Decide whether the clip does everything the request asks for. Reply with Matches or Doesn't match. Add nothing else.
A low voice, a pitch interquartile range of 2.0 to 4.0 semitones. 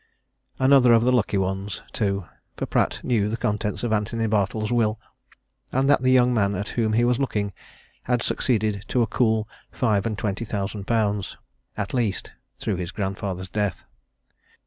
Matches